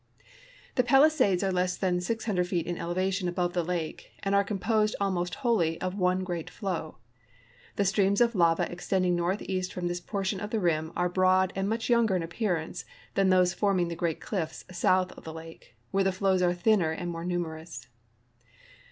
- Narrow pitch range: Yes, narrow, 2.2 semitones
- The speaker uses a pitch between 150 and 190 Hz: Yes, medium, 185 Hz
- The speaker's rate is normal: Yes, average, 185 wpm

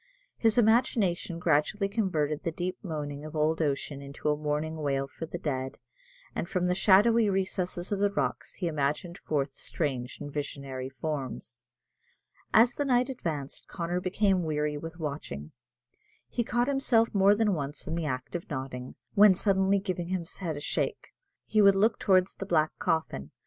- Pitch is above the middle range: No, medium, 170 Hz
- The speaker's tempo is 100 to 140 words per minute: No, average, 170 wpm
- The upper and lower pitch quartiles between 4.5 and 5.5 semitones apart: Yes, average, 5.1 semitones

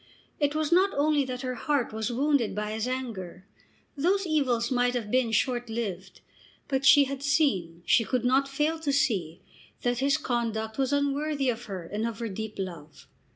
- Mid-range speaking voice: No, very high, 250 Hz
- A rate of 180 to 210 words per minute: Yes, average, 185 wpm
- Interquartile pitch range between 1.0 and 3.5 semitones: No, average, 4.4 semitones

